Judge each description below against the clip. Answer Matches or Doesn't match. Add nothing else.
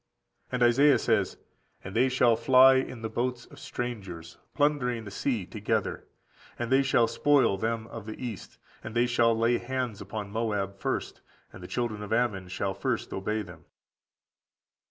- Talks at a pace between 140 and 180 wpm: Matches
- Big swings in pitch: Doesn't match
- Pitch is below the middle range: Matches